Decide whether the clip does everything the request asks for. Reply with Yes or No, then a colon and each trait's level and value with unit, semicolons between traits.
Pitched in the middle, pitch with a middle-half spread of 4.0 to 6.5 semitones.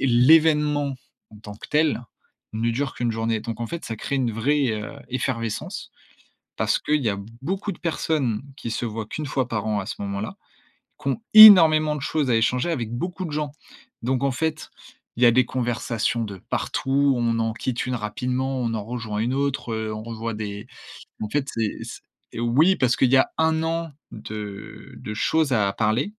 No: low, 125 Hz; average, 4.6 semitones